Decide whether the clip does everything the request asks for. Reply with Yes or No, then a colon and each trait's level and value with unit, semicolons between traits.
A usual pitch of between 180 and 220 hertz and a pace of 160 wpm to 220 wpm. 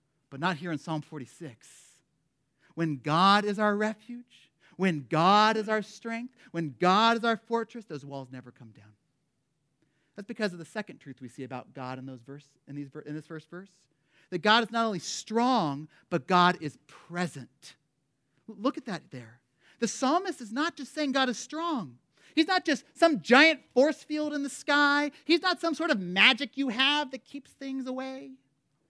Yes: medium, 185 Hz; average, 185 wpm